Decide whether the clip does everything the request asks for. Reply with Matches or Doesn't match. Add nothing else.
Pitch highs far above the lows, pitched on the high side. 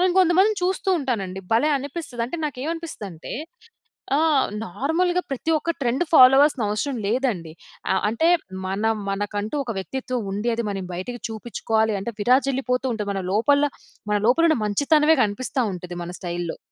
Matches